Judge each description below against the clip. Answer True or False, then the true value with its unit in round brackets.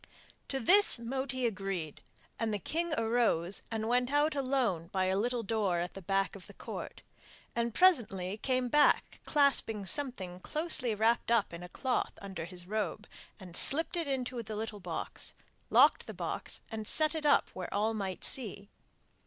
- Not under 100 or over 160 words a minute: False (170 wpm)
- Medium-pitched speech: False (225 Hz)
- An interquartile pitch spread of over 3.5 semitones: True (5.2 semitones)